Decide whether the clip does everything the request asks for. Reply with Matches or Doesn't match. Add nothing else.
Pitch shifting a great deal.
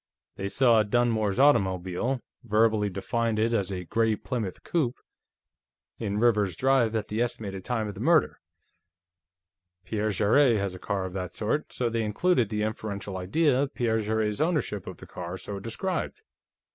Doesn't match